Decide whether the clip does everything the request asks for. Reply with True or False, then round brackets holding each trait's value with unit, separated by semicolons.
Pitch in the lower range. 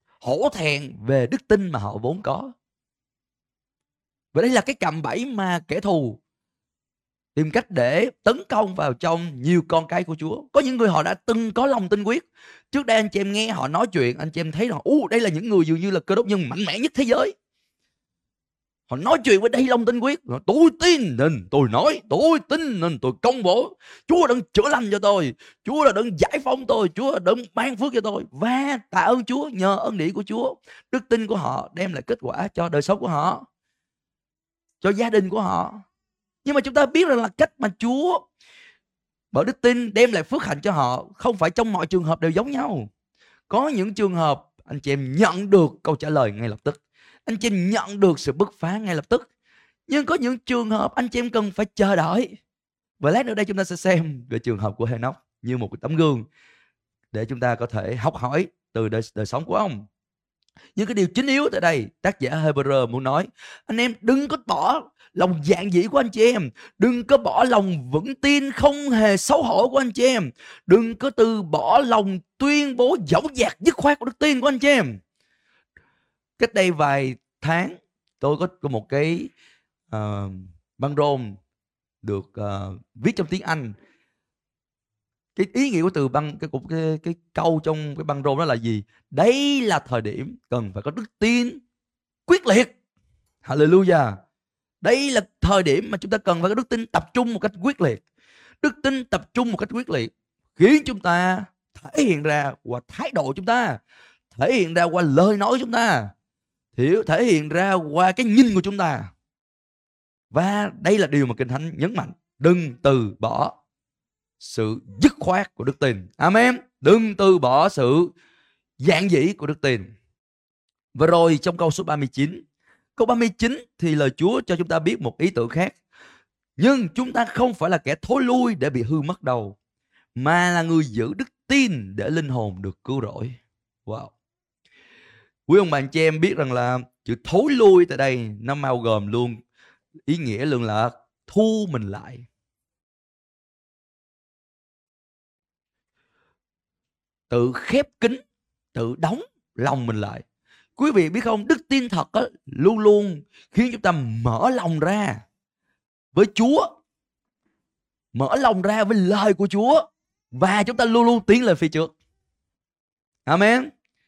False (185 Hz)